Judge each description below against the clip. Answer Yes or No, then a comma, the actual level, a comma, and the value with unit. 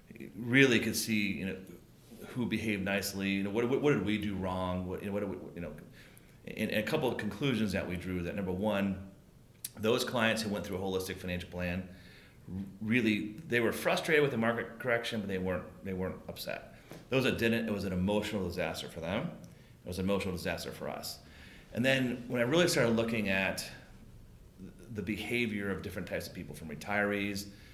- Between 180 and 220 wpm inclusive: Yes, average, 195 wpm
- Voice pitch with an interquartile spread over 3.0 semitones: Yes, average, 3.6 semitones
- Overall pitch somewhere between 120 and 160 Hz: No, low, 100 Hz